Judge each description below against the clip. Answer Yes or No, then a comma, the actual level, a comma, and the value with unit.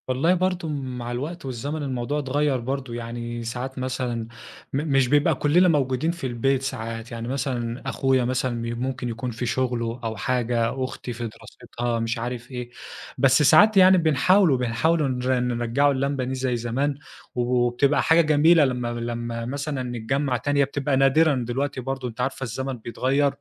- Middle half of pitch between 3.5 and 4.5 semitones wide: No, average, 2.8 semitones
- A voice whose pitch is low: Yes, low, 130 Hz